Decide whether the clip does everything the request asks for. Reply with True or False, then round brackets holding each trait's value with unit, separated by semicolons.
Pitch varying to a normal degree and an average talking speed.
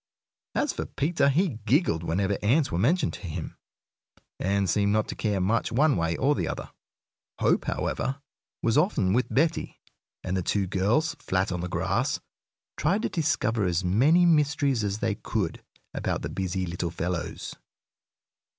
False (7.6 semitones; 160 wpm)